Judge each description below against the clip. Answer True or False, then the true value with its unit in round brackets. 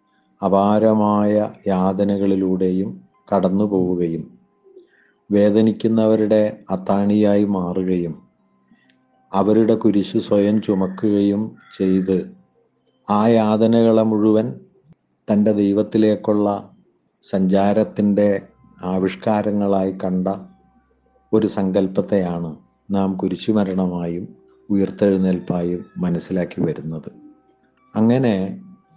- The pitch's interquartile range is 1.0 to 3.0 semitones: True (2.4 semitones)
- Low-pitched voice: True (100 Hz)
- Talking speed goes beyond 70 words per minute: False (60 wpm)